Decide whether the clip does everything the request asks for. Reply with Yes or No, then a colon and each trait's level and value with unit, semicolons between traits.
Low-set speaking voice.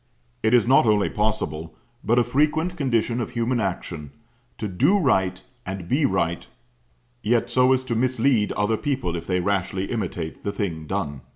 Yes: low, 110 Hz